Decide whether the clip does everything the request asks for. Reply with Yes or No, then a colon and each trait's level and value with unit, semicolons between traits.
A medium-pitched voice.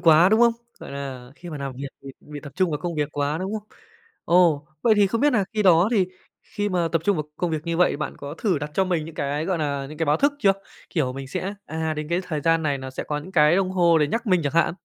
Yes: medium, 165 Hz